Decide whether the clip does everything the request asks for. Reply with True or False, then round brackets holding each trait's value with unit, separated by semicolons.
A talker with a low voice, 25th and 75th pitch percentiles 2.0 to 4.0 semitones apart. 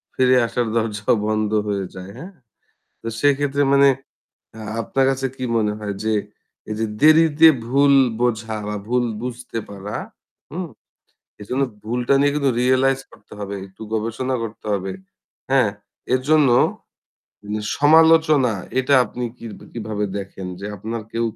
False (125 Hz; 4.5 semitones)